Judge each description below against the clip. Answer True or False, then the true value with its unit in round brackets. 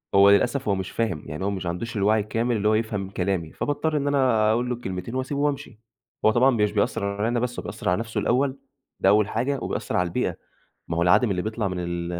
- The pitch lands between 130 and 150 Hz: False (110 Hz)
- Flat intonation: False (4.3 semitones)